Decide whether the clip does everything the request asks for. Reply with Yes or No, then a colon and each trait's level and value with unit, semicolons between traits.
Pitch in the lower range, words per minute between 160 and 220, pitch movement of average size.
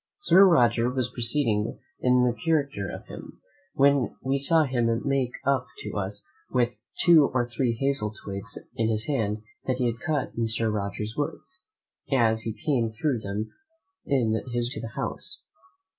Yes: low, 120 Hz; average, 170 wpm; average, 3.8 semitones